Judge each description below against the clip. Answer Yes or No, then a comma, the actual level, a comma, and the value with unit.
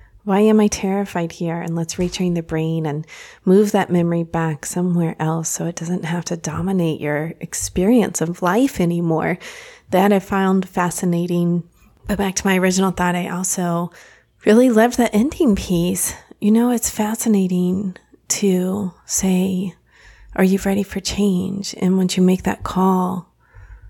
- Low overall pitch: No, medium, 185 Hz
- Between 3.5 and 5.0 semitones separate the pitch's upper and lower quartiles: No, narrow, 2.6 semitones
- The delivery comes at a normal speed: Yes, average, 155 wpm